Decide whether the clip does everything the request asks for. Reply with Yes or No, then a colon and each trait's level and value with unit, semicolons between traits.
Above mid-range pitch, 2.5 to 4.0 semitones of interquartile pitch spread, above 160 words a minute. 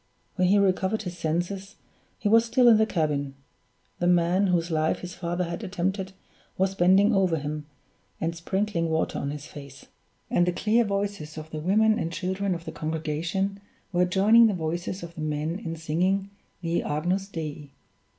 No: medium, 175 Hz; average, 3.5 semitones; average, 175 wpm